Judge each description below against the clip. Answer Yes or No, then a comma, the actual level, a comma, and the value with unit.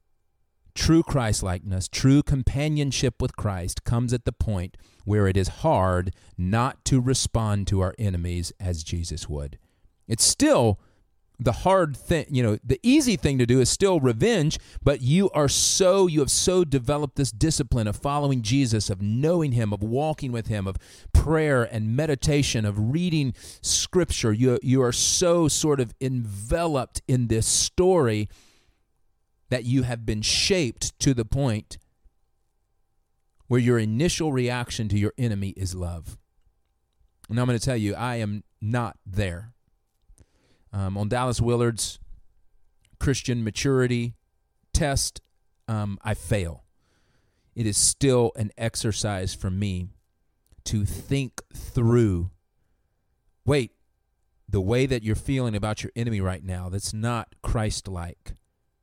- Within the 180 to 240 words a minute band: No, average, 140 wpm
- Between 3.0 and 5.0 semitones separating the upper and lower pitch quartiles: No, wide, 5.4 semitones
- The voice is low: Yes, low, 115 Hz